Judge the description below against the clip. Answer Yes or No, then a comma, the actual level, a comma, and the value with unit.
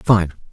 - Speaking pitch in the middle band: No, very low, 95 Hz